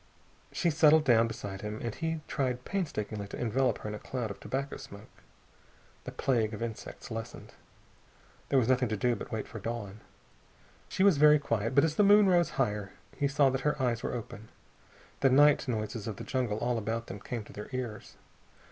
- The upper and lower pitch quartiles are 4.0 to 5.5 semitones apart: Yes, average, 4.6 semitones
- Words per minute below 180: No, average, 200 wpm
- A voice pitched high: No, low, 120 Hz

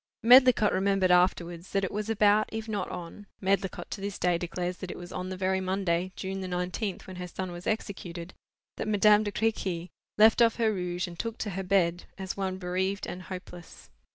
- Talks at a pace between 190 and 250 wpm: Yes, average, 200 wpm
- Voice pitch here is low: No, high, 190 Hz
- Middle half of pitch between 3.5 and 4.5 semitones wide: No, narrow, 2.4 semitones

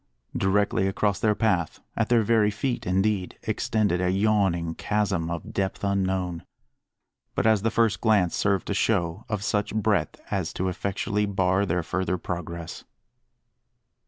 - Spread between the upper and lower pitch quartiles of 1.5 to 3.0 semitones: Yes, average, 2.7 semitones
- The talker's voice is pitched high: No, low, 100 Hz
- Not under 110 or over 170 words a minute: Yes, average, 145 wpm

